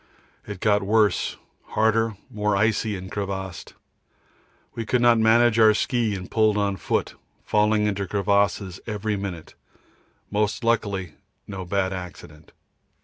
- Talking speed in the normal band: No, slow, 130 wpm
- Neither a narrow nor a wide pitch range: No, narrow, 2.3 semitones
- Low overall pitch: Yes, low, 105 Hz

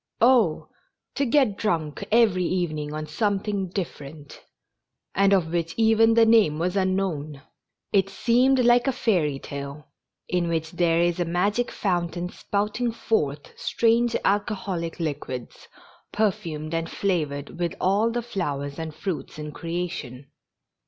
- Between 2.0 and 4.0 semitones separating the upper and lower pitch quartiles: No, wide, 5.4 semitones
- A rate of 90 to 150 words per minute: Yes, average, 140 wpm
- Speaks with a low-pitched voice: No, medium, 180 Hz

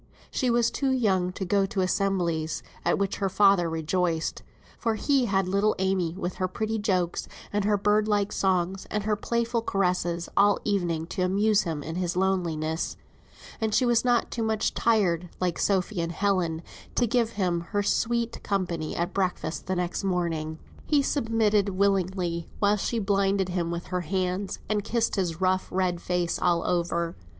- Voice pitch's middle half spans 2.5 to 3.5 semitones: Yes, average, 3.0 semitones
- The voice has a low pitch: No, high, 190 Hz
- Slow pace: No, average, 175 wpm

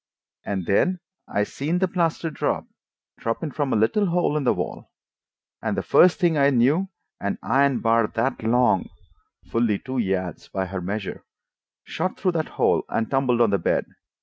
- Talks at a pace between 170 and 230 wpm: Yes, average, 175 wpm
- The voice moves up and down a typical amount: No, wide, 7.2 semitones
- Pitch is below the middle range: Yes, low, 125 Hz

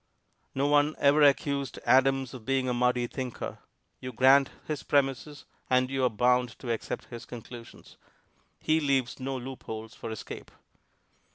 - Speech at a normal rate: Yes, average, 150 wpm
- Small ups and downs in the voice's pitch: Yes, narrow, 2.1 semitones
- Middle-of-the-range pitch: No, low, 130 Hz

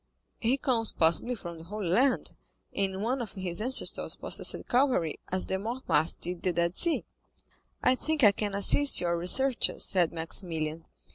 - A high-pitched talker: Yes, high, 195 Hz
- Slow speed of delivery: No, average, 160 wpm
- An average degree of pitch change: No, wide, 6.3 semitones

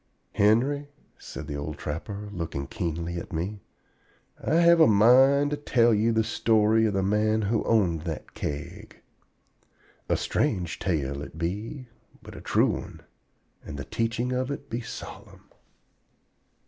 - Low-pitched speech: Yes, low, 105 Hz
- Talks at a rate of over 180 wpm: No, average, 150 wpm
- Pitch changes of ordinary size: No, wide, 5.9 semitones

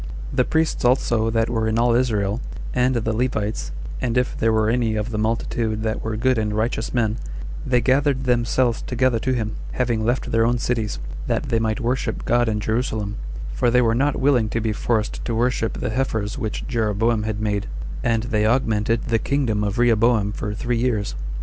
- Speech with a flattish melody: Yes, narrow, 2.1 semitones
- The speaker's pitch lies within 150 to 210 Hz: No, low, 115 Hz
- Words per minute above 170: Yes, average, 195 wpm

